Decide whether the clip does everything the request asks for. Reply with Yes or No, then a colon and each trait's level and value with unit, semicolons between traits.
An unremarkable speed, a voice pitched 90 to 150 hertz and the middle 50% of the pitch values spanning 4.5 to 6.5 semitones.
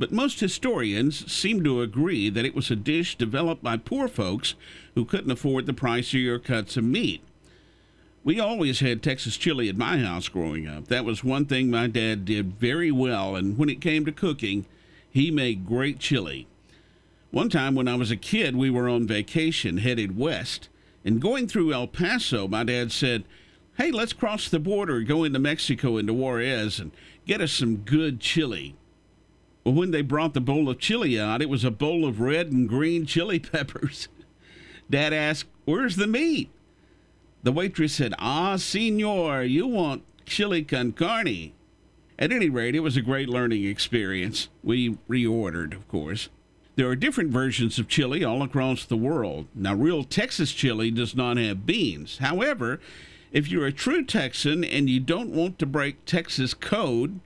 Yes: average, 180 wpm; low, 135 Hz; wide, 5.6 semitones